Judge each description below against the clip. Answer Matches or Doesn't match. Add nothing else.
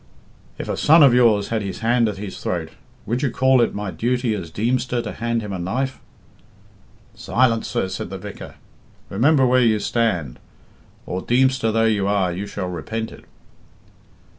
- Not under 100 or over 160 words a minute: Doesn't match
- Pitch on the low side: Matches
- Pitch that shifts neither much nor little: Matches